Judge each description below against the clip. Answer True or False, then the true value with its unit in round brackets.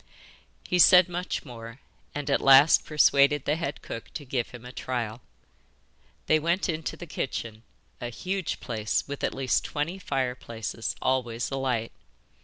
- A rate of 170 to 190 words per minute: False (150 wpm)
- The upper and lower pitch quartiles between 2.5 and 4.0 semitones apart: False (4.5 semitones)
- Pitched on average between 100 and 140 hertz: True (135 Hz)